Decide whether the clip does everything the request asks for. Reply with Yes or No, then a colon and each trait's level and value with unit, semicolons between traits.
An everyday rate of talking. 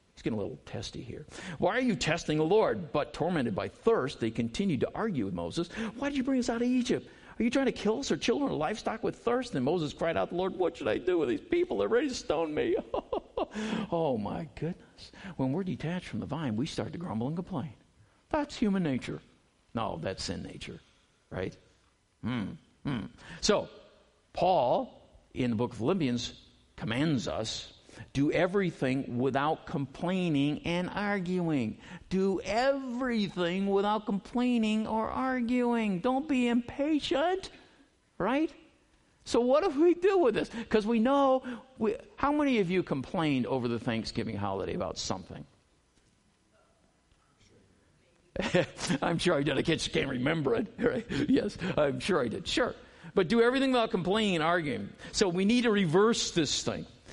Yes: average, 170 wpm